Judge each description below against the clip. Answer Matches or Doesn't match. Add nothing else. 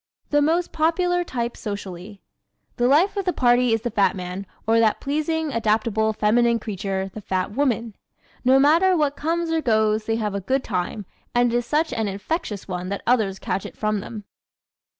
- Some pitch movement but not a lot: Doesn't match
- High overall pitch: Matches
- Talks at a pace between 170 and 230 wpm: Matches